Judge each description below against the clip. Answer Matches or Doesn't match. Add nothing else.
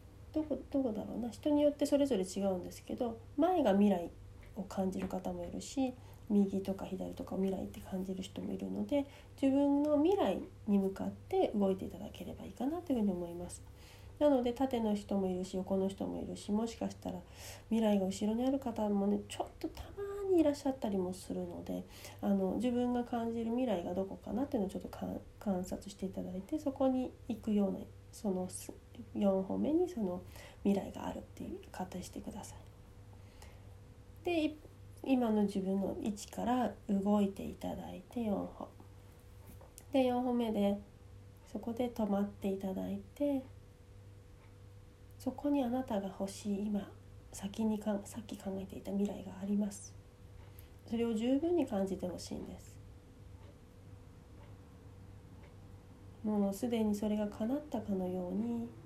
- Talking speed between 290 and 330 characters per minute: Matches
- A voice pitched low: Doesn't match